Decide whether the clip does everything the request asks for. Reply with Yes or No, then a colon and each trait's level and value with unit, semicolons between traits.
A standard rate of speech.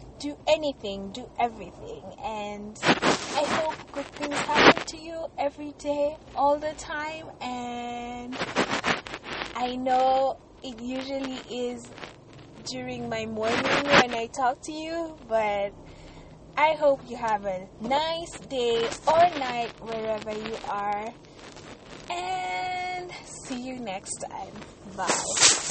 No: slow, 115 wpm